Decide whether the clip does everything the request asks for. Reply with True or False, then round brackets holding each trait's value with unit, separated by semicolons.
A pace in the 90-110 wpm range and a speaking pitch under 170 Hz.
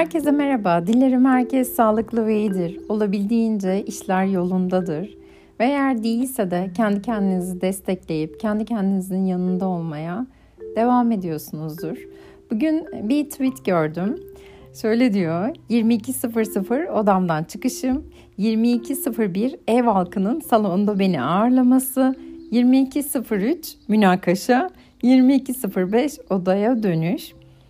False (95 wpm; 220 Hz)